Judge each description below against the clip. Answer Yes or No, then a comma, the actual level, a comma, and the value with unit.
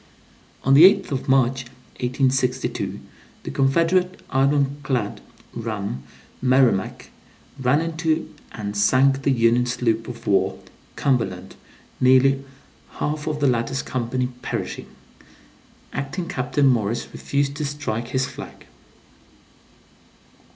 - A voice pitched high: No, low, 130 Hz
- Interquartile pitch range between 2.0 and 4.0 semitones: Yes, average, 2.8 semitones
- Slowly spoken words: Yes, slow, 110 wpm